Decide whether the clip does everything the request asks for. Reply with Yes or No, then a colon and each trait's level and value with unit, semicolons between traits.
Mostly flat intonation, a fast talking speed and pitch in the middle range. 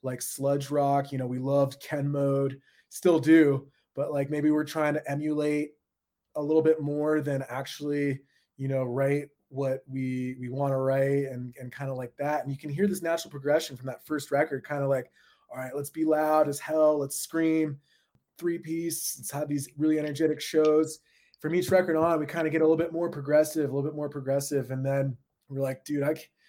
Yes: narrow, 2.2 semitones; fast, 215 wpm; medium, 145 Hz